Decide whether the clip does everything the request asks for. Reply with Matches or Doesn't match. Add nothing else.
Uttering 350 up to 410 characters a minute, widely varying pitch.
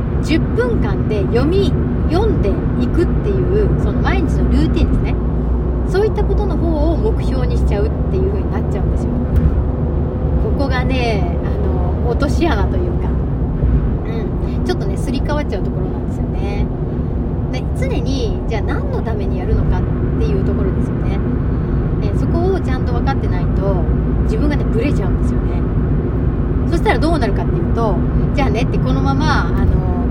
Doesn't match